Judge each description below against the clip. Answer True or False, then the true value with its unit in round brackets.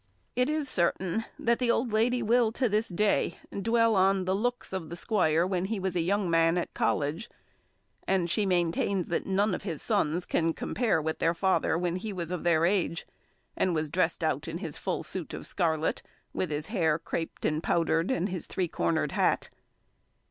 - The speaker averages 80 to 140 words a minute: False (195 wpm)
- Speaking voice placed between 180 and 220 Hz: True (185 Hz)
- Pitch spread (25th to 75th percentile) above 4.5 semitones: False (4.2 semitones)